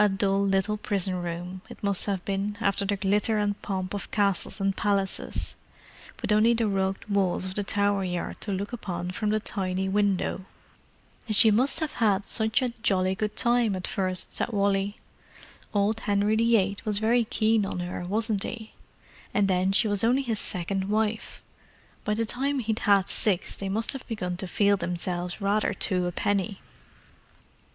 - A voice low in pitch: No, high, 200 Hz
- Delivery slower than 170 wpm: No, average, 175 wpm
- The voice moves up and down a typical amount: No, narrow, 2.2 semitones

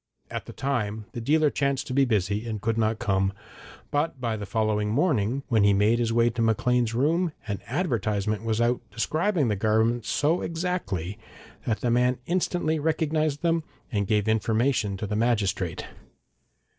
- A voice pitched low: Yes, low, 115 Hz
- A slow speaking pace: No, average, 170 wpm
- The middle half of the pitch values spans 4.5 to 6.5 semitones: Yes, average, 4.9 semitones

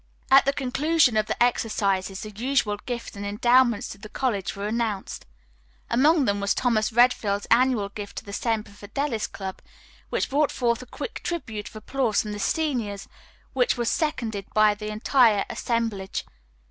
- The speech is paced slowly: No, average, 165 wpm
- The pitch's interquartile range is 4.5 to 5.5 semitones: No, average, 3.7 semitones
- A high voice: Yes, high, 225 Hz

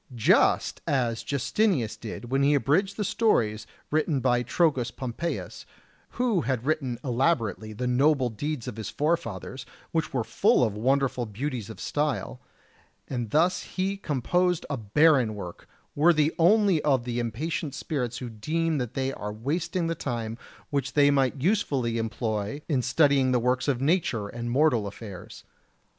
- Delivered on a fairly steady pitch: No, average, 4.9 semitones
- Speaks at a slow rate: No, average, 150 wpm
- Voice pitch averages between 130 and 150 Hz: Yes, low, 135 Hz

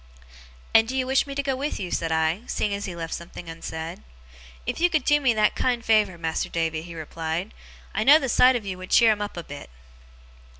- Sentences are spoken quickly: Yes, fast, 230 wpm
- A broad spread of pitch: Yes, wide, 7.6 semitones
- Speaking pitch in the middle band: No, high, 200 Hz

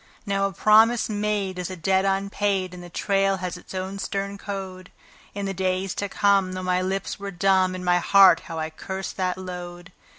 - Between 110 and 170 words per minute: No, average, 200 wpm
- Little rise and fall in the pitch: Yes, narrow, 1.4 semitones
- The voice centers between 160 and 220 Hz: Yes, high, 190 Hz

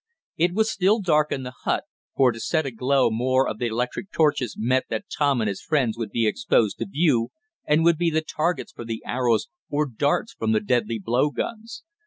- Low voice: Yes, low, 130 Hz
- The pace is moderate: No, fast, 210 wpm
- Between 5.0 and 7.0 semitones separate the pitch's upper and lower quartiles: Yes, wide, 5.4 semitones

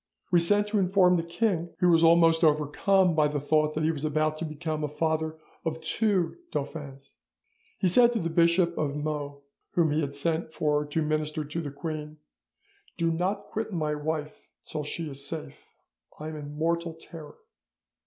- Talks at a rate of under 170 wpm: No, average, 185 wpm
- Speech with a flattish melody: Yes, narrow, 2.1 semitones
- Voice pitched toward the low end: No, medium, 160 Hz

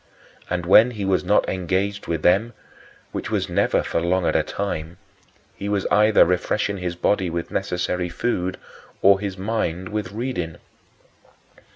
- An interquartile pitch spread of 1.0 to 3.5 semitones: Yes, narrow, 2.6 semitones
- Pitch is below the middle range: Yes, very low, 95 Hz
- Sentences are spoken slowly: No, average, 155 wpm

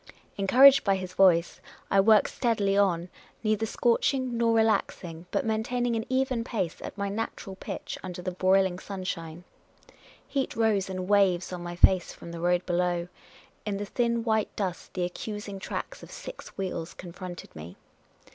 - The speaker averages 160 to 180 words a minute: Yes, average, 165 wpm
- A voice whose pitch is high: Yes, high, 195 Hz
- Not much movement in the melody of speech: No, average, 3.8 semitones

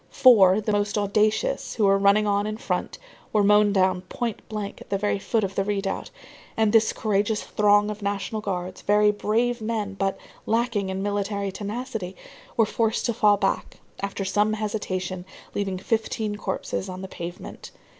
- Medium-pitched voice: No, high, 205 Hz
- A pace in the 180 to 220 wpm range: No, average, 170 wpm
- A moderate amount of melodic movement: No, narrow, 1.6 semitones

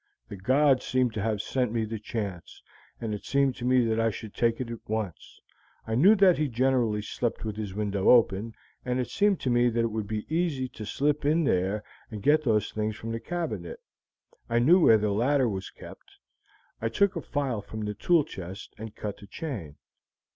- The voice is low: Yes, low, 115 Hz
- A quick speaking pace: Yes, fast, 210 wpm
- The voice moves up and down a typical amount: Yes, average, 4.0 semitones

